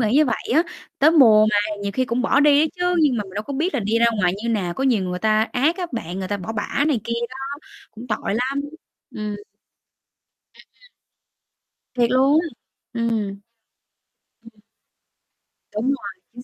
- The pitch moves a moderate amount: Yes, average, 4.9 semitones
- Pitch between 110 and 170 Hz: No, high, 235 Hz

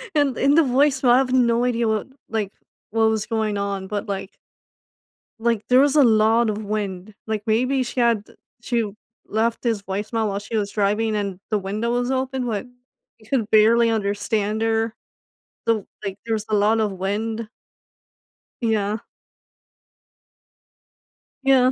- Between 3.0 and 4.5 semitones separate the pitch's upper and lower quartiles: No, narrow, 2.4 semitones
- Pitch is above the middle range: Yes, high, 220 Hz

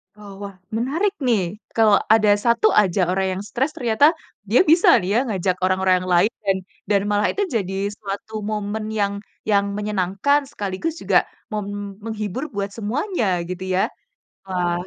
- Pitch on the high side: Yes, high, 205 Hz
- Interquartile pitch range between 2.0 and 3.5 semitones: Yes, average, 3.1 semitones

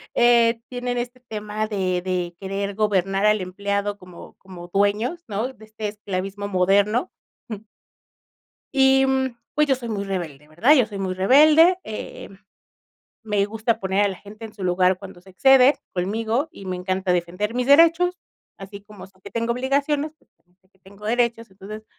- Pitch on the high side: Yes, high, 210 Hz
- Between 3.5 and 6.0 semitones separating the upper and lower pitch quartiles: Yes, average, 4.2 semitones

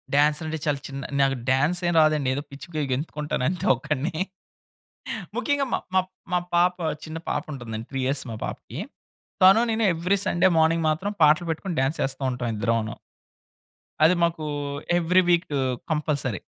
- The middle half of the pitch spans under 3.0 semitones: No, average, 4.1 semitones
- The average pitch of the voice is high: No, medium, 155 Hz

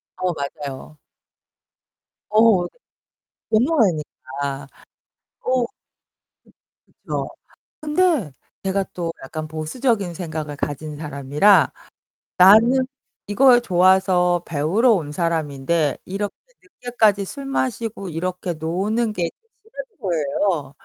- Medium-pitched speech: Yes, medium, 180 Hz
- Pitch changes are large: Yes, wide, 6.3 semitones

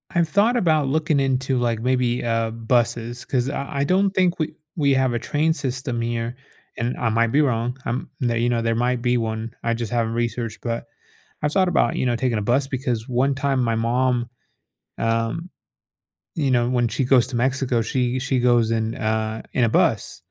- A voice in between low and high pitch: No, low, 120 Hz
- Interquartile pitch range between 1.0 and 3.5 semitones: Yes, narrow, 2.6 semitones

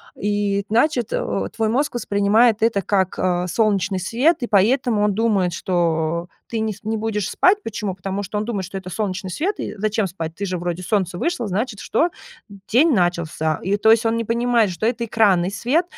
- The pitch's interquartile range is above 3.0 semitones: Yes, average, 3.8 semitones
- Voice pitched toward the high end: Yes, high, 205 Hz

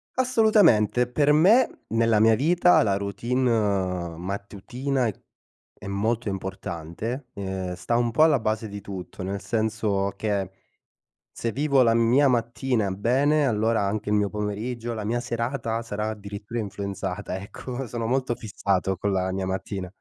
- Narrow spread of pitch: No, average, 3.7 semitones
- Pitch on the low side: Yes, low, 110 Hz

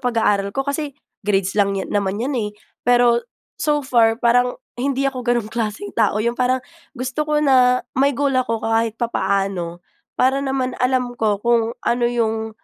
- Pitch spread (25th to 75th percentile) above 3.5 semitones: No, average, 2.9 semitones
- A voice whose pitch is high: Yes, high, 240 Hz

